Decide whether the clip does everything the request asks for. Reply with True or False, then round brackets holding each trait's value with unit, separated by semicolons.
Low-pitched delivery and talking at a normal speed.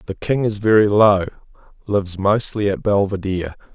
True (100 Hz; 145 wpm)